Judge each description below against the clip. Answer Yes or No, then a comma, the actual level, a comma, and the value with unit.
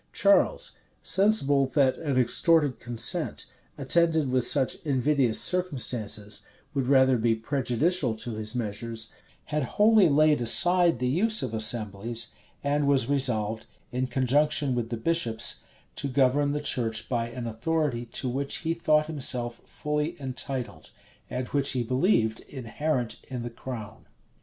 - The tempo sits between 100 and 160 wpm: Yes, average, 140 wpm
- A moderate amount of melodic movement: Yes, average, 4.1 semitones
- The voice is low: Yes, low, 130 Hz